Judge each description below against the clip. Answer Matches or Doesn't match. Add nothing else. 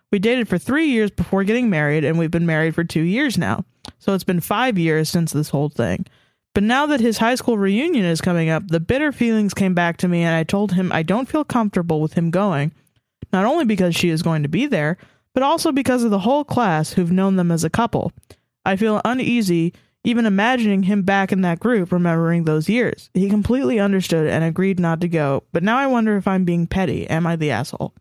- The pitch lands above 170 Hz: Matches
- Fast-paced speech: Matches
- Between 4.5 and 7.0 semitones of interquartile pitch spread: Matches